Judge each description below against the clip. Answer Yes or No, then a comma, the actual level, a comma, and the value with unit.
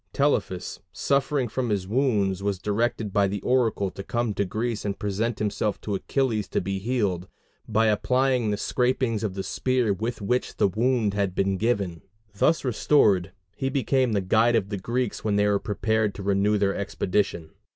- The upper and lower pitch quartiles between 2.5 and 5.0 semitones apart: Yes, average, 3.5 semitones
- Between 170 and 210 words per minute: Yes, average, 180 wpm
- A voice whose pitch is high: No, low, 105 Hz